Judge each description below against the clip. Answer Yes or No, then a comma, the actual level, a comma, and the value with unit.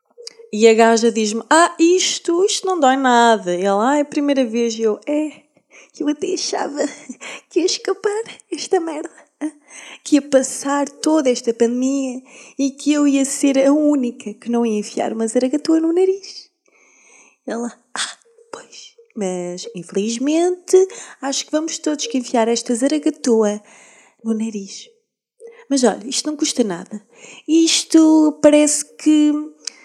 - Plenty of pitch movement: Yes, wide, 5.7 semitones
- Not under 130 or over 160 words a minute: Yes, average, 150 wpm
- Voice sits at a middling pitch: No, very high, 285 Hz